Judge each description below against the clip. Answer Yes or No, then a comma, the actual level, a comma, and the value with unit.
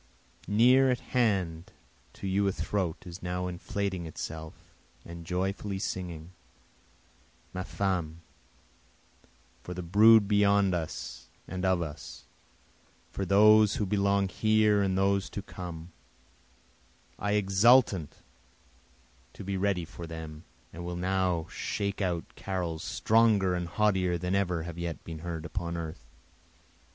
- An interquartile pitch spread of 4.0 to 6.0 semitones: No, average, 2.9 semitones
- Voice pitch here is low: Yes, very low, 95 Hz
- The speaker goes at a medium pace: No, slow, 125 wpm